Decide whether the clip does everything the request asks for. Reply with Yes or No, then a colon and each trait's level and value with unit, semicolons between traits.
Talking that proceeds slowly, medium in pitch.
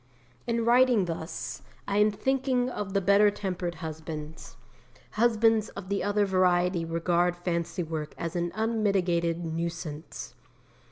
Yes: slow, 125 wpm; medium, 180 Hz